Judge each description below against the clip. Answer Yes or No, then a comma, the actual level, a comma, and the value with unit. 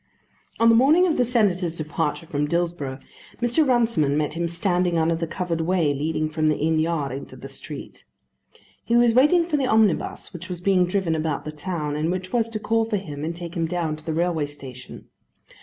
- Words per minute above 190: Yes, fast, 205 wpm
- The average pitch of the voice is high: No, medium, 170 Hz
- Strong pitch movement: Yes, wide, 5.7 semitones